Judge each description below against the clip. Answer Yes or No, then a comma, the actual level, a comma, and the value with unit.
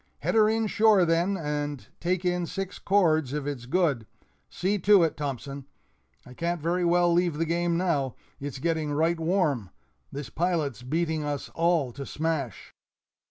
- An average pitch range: Yes, average, 3.6 semitones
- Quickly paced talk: No, average, 160 wpm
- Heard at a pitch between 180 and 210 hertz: No, medium, 165 Hz